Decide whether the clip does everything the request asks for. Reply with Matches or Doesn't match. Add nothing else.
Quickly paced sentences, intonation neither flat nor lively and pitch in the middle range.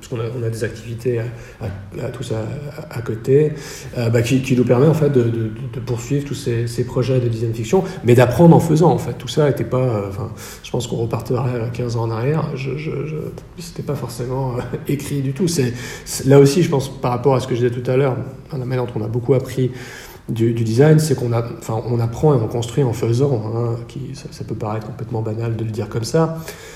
Doesn't match